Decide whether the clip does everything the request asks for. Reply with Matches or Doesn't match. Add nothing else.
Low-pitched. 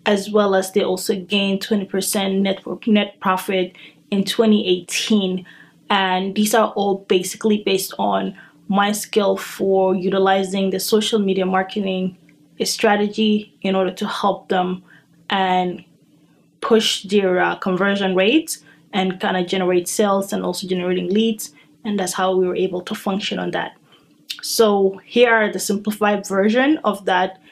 Doesn't match